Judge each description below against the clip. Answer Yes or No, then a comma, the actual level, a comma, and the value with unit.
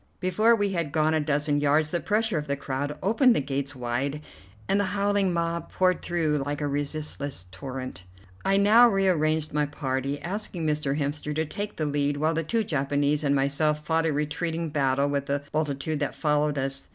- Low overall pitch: No, medium, 150 Hz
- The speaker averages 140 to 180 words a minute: No, average, 195 wpm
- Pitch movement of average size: Yes, average, 3.1 semitones